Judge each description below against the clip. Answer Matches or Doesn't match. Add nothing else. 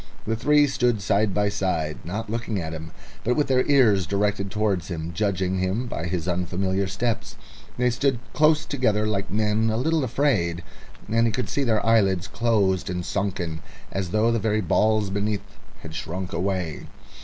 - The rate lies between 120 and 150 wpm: Doesn't match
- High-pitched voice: Doesn't match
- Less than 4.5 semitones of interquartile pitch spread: Matches